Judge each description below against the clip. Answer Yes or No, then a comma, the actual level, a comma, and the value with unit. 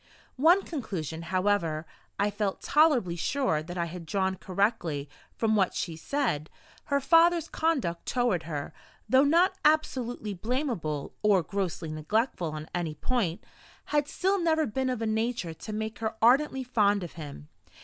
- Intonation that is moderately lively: No, wide, 7.7 semitones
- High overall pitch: Yes, high, 210 Hz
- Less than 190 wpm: Yes, average, 150 wpm